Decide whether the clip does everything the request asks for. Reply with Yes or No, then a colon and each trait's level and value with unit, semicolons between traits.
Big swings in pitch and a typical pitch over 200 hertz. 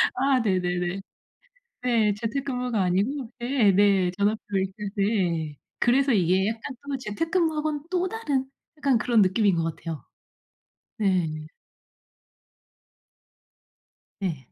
Yes: wide, 6.2 semitones; high, 210 Hz